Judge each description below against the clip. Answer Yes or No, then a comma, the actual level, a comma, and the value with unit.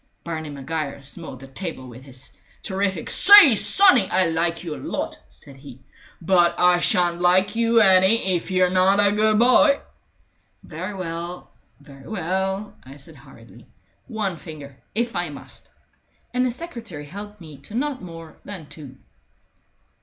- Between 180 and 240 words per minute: No, average, 155 wpm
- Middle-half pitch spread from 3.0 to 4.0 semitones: No, average, 4.9 semitones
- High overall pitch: No, medium, 180 Hz